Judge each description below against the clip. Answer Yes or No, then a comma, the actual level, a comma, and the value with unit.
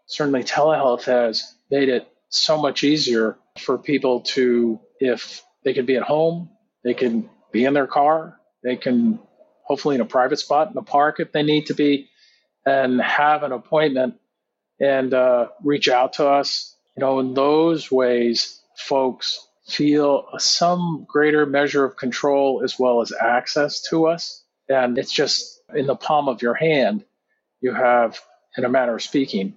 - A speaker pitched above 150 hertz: No, medium, 140 Hz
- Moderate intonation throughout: Yes, average, 3.4 semitones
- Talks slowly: No, average, 165 wpm